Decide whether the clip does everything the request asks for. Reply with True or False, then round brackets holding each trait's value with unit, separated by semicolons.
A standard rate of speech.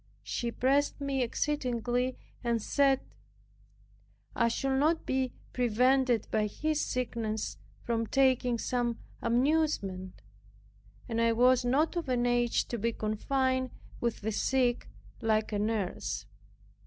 False (120 wpm)